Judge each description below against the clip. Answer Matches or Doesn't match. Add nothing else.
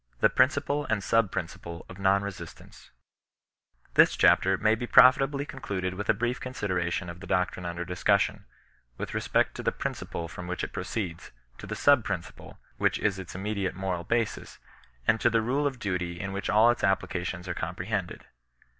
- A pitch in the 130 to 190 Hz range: Doesn't match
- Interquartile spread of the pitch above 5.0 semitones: Doesn't match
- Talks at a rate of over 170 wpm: Matches